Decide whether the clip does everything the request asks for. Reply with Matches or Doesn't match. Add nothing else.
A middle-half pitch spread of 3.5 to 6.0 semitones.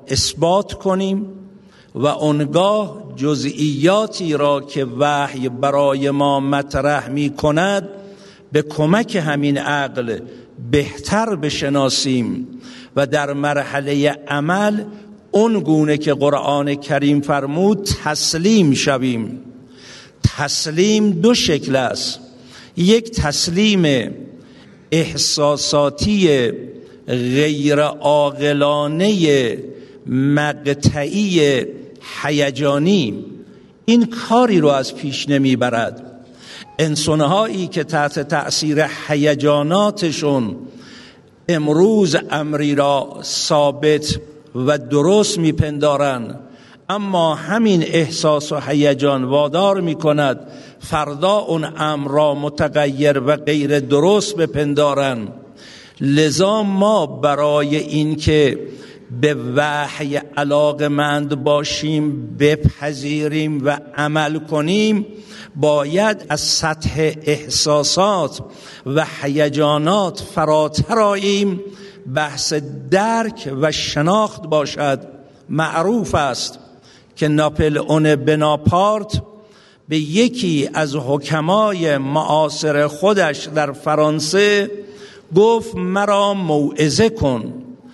Matches